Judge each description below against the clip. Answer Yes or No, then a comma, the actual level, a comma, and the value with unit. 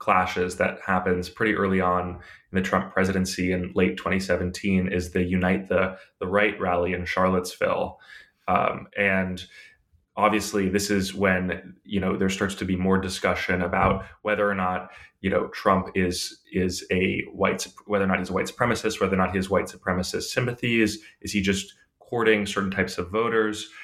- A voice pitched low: Yes, very low, 95 Hz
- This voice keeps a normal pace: Yes, average, 180 wpm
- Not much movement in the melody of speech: Yes, narrow, 1.7 semitones